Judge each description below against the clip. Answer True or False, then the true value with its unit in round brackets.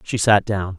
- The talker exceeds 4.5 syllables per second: False (4.4 syllables/s)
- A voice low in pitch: True (100 Hz)